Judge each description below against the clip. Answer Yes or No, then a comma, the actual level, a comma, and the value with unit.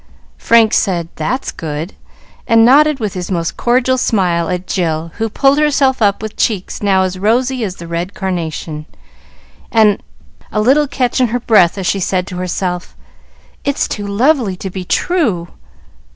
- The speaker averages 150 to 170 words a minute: Yes, average, 165 wpm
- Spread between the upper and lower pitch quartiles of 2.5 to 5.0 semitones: No, wide, 5.5 semitones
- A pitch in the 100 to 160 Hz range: No, high, 200 Hz